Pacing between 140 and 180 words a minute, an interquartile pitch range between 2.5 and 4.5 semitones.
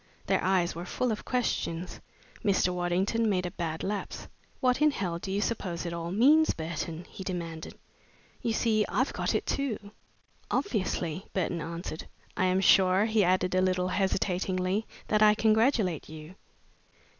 Yes: average, 155 wpm; average, 3.6 semitones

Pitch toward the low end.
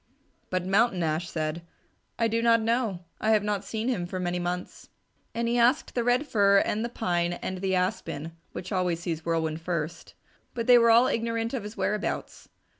No: high, 200 Hz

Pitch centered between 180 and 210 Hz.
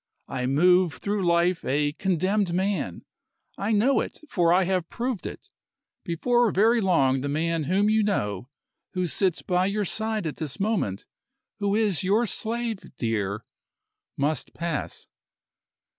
Yes: medium, 185 Hz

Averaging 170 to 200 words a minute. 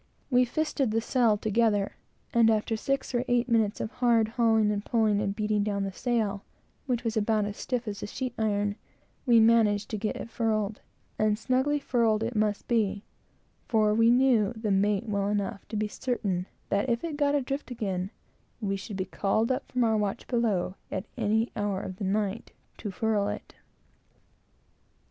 Yes: average, 175 wpm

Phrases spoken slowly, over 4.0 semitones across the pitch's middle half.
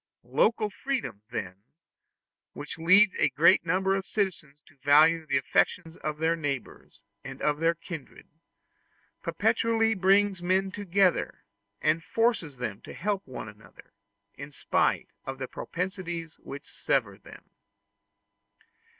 Yes: slow, 125 wpm; wide, 5.4 semitones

